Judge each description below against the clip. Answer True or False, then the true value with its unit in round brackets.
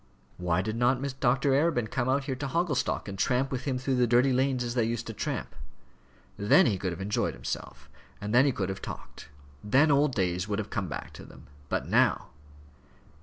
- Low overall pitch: True (120 Hz)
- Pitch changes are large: False (4.7 semitones)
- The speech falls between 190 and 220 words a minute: True (205 wpm)